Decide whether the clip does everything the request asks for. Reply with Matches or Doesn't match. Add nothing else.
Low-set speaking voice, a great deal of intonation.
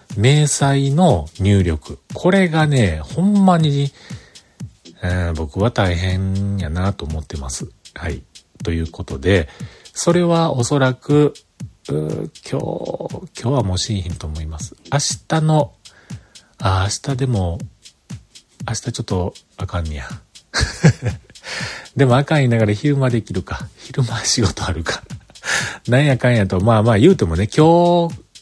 Matches